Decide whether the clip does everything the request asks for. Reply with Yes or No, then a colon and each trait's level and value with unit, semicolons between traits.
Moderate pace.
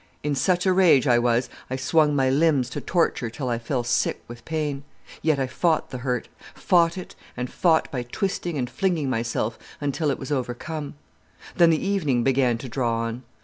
Yes: average, 190 wpm